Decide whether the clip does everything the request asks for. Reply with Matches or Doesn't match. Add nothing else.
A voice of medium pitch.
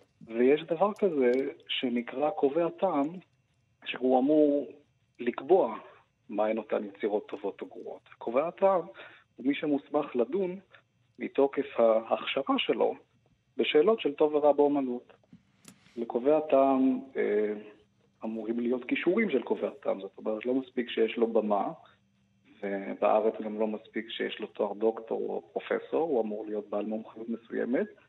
Doesn't match